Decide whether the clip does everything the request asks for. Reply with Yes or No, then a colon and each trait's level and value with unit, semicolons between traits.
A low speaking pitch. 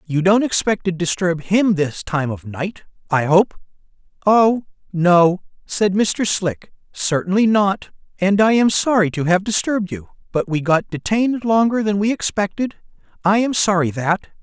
No: high, 190 Hz